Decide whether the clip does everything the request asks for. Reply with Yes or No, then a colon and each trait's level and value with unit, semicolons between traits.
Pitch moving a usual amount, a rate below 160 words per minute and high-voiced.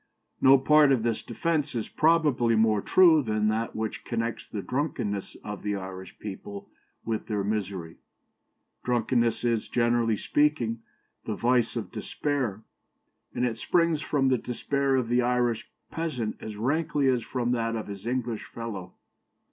No: average, 3.6 semitones; average, 150 wpm; low, 120 Hz